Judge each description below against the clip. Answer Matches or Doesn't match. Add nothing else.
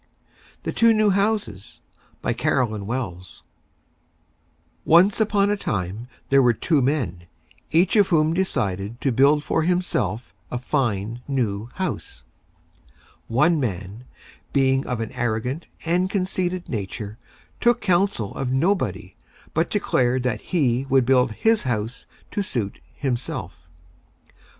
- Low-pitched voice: Matches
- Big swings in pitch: Matches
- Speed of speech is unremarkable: Doesn't match